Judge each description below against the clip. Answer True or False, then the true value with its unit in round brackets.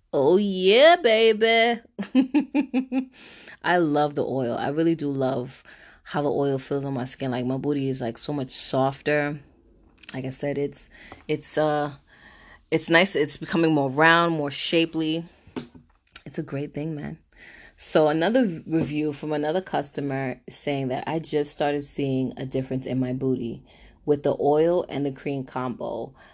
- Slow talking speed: False (155 wpm)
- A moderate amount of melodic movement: True (3.7 semitones)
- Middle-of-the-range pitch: True (145 Hz)